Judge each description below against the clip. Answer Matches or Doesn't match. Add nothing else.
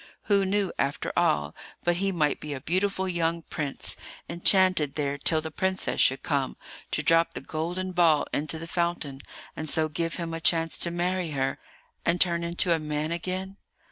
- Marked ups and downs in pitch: Doesn't match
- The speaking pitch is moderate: Matches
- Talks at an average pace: Matches